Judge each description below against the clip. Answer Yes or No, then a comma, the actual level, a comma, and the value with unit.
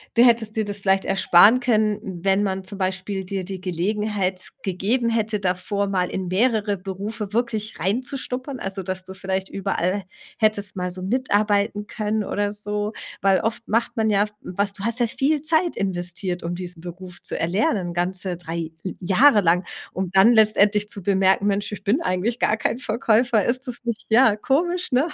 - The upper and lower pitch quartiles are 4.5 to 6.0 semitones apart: No, average, 2.9 semitones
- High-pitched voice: Yes, high, 205 Hz